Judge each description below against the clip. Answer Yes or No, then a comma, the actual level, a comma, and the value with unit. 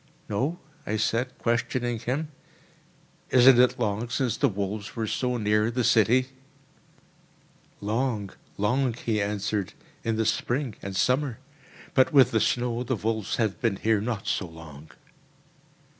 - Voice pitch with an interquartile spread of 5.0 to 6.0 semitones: No, average, 3.2 semitones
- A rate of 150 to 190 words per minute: No, average, 140 wpm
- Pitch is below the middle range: Yes, low, 115 Hz